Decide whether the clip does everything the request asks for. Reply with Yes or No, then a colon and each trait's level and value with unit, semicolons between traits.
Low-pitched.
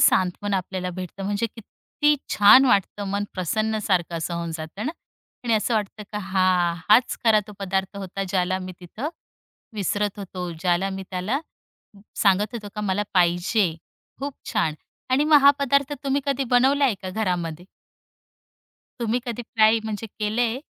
No: high, 205 Hz